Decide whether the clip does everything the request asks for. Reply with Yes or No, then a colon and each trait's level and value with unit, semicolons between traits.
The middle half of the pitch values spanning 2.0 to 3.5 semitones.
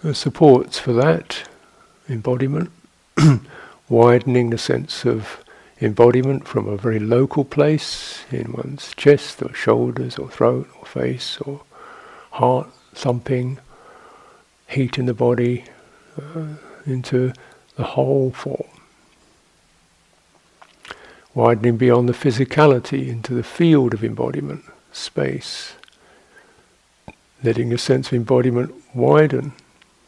Yes: average, 3.2 semitones